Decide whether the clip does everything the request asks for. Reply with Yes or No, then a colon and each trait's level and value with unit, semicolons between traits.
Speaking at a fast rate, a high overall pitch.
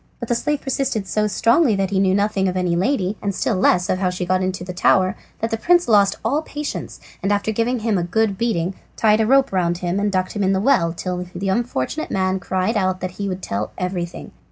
Yes: fast, 240 wpm; high, 195 Hz